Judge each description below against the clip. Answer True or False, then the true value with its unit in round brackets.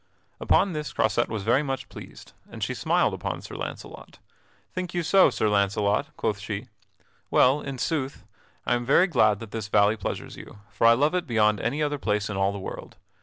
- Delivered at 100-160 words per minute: False (200 wpm)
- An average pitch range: False (5.8 semitones)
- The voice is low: True (115 Hz)